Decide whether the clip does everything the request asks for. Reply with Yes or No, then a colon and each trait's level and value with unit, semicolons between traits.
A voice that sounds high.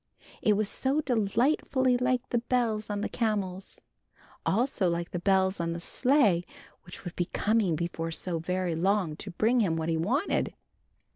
Yes: high, 200 Hz